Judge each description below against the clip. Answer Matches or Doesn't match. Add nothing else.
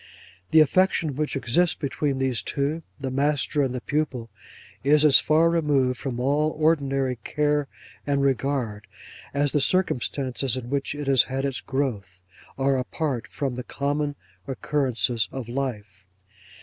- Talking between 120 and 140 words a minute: Matches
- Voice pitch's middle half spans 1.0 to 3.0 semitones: Matches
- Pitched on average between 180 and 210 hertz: Doesn't match